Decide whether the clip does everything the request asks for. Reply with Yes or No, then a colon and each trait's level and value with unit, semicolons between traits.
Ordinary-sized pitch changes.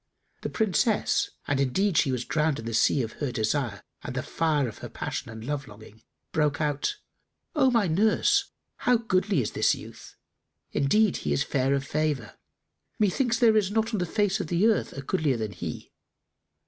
No: wide, 8.8 semitones